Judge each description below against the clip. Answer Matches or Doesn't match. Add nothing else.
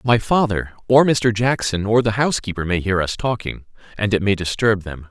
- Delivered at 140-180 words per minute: Doesn't match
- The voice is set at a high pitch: Doesn't match